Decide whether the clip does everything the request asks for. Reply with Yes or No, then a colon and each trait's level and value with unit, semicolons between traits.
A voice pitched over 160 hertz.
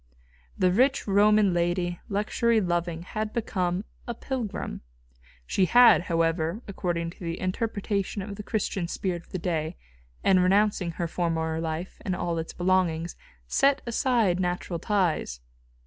Yes: medium, 185 Hz